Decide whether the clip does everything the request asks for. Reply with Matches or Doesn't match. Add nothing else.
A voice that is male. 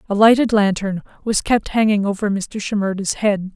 Doesn't match